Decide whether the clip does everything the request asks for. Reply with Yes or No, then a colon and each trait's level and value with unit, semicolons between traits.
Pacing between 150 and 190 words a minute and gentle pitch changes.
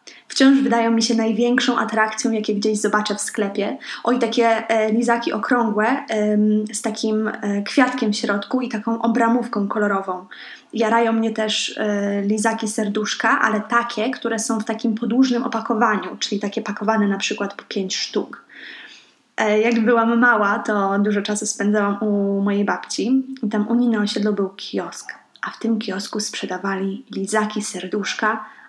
Yes: average, 155 wpm; narrow, 1.9 semitones